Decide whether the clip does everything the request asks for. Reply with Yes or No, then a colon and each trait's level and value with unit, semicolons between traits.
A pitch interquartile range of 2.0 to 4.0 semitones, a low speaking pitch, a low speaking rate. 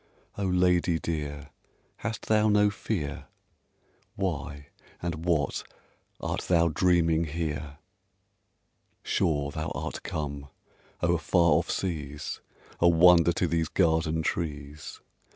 Yes: average, 3.0 semitones; very low, 80 Hz; slow, 110 wpm